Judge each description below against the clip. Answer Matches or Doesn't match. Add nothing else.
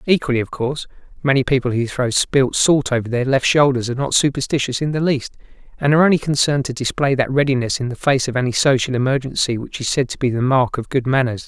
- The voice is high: Doesn't match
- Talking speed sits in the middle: Doesn't match